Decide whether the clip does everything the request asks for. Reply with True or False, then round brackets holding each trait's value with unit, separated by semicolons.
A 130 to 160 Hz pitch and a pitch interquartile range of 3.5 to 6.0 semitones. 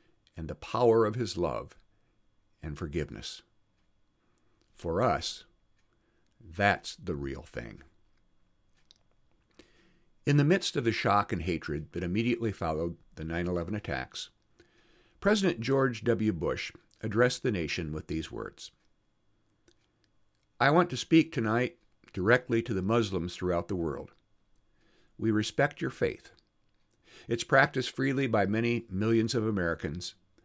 False (110 Hz; 4.6 semitones)